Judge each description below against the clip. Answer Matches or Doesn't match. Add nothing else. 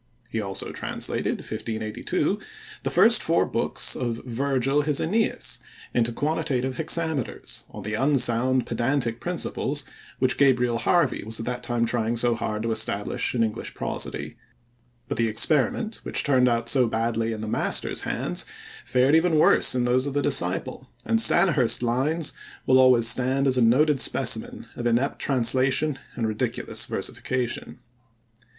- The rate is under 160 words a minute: Matches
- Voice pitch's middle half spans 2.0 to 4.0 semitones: Matches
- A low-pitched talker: Matches